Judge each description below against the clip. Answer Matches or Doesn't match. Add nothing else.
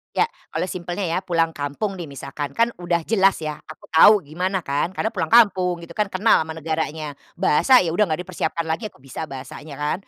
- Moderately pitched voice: Matches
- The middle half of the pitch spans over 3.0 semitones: Matches